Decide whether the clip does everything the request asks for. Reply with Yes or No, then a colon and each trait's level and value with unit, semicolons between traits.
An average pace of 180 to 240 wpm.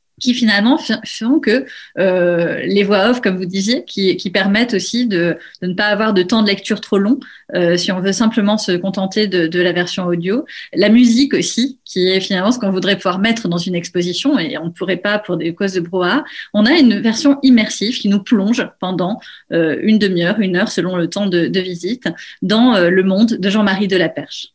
Yes: fast, 220 wpm